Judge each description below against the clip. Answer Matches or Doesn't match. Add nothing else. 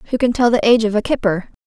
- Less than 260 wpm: Doesn't match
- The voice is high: Matches